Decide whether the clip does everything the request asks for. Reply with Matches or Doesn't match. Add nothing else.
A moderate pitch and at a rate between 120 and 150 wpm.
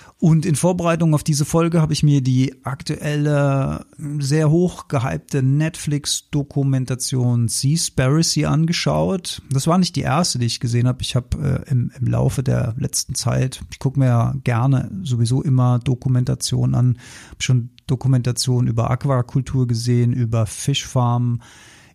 Doesn't match